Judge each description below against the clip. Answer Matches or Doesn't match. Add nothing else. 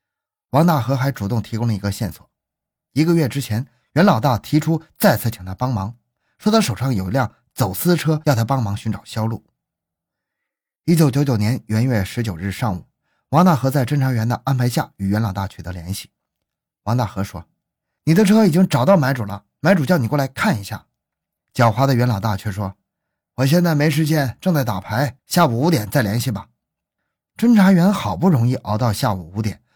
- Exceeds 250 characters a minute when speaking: Matches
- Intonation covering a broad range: Matches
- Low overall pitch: Matches